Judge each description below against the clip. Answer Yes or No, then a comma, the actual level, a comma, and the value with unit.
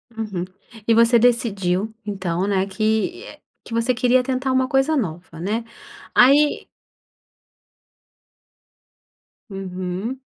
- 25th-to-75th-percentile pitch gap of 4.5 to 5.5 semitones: Yes, average, 4.8 semitones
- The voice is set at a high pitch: Yes, high, 225 Hz